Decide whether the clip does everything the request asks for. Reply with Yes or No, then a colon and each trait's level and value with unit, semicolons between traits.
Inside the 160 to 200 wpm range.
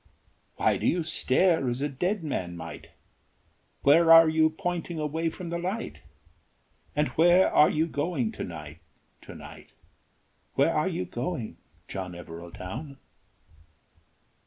No: slow, 135 wpm